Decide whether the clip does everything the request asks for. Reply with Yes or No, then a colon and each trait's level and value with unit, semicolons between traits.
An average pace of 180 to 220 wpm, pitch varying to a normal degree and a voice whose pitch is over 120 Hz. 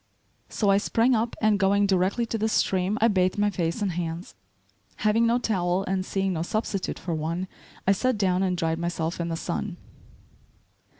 Yes: average, 185 wpm; average, 3.2 semitones; high, 190 Hz